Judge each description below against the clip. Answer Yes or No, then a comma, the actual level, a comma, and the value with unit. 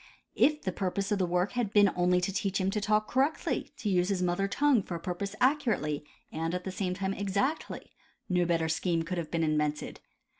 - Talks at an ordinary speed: No, fast, 225 wpm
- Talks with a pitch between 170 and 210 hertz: Yes, medium, 185 Hz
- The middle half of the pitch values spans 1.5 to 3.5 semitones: Yes, average, 2.9 semitones